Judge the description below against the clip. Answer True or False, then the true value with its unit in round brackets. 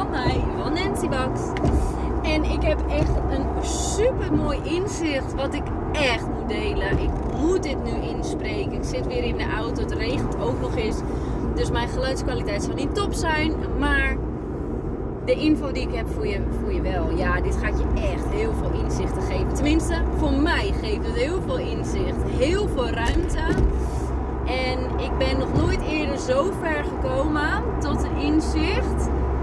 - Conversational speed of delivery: True (170 wpm)